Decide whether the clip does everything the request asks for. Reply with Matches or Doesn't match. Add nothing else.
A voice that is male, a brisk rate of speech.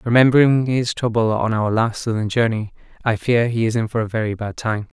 Matches